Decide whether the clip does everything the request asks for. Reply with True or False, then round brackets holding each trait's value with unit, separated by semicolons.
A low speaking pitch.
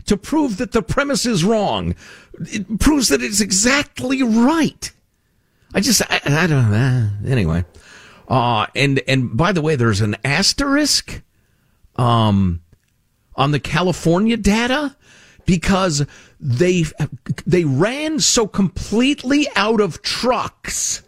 False (170 Hz)